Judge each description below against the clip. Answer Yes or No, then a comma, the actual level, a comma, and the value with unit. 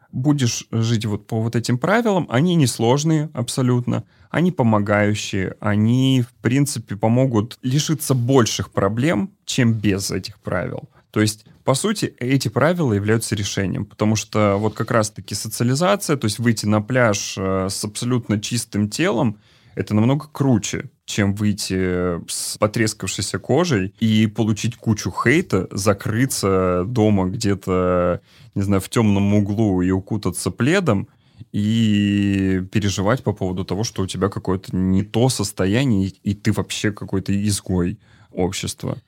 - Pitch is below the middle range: Yes, low, 110 Hz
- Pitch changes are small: No, average, 4.0 semitones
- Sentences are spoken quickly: No, average, 135 wpm